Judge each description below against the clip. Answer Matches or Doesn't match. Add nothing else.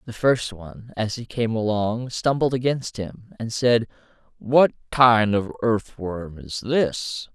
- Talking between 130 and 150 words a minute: Matches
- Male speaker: Matches